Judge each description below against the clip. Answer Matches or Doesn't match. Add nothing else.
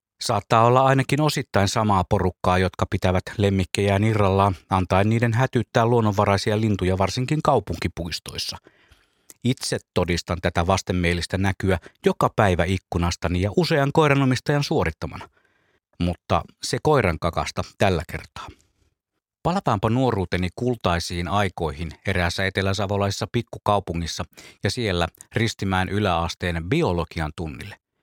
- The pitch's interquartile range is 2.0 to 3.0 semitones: Doesn't match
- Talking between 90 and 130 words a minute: Matches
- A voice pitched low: Matches